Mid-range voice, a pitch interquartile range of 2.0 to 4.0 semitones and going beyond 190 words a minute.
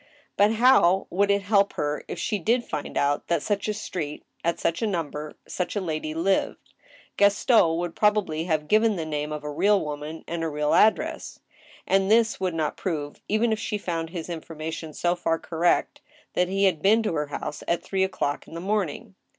No: medium, 175 Hz; average, 4.4 semitones; fast, 205 wpm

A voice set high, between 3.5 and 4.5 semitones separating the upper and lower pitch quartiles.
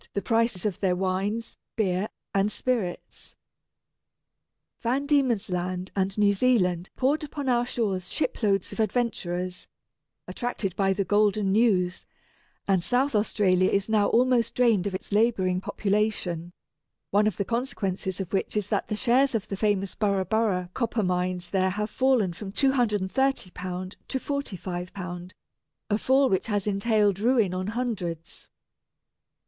Yes: high, 205 Hz; average, 3.9 semitones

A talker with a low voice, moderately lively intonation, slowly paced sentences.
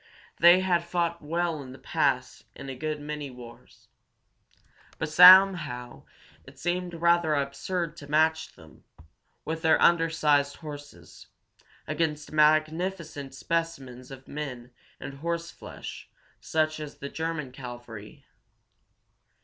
No: medium, 155 Hz; average, 3.5 semitones; slow, 115 wpm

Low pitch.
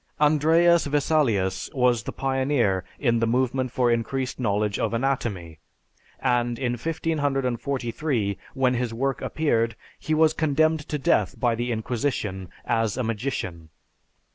Yes: low, 125 Hz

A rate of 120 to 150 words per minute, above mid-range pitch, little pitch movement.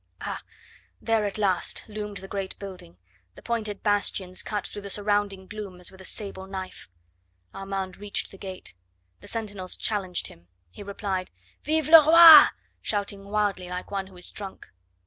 No: average, 165 wpm; high, 200 Hz; narrow, 1.8 semitones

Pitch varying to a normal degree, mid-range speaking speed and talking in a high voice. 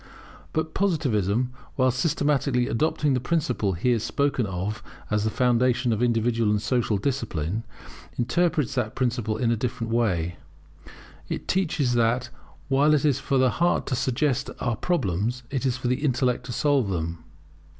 No: average, 3.9 semitones; average, 155 wpm; low, 125 Hz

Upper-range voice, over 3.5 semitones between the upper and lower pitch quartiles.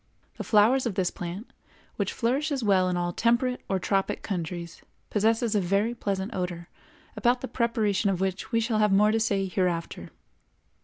Yes: high, 205 Hz; average, 3.9 semitones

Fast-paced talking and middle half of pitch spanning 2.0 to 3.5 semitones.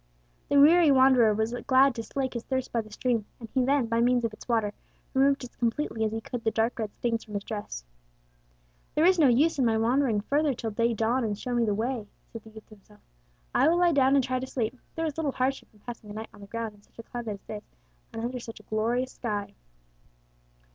Yes: fast, 245 wpm; average, 3.2 semitones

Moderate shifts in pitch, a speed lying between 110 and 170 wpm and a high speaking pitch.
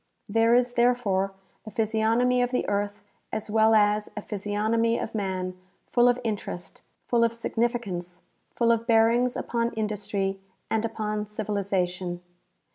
No: narrow, 2.3 semitones; average, 140 wpm; high, 220 Hz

